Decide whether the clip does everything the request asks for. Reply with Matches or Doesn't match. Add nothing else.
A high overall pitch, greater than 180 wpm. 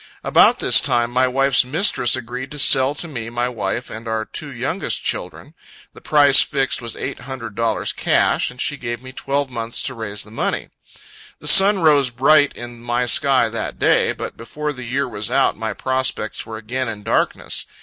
Doesn't match